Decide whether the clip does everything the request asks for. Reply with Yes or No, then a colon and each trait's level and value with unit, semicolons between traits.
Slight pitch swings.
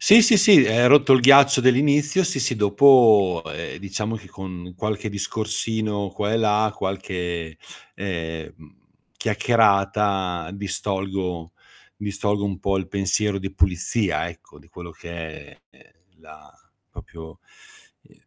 No: average, 3.8 semitones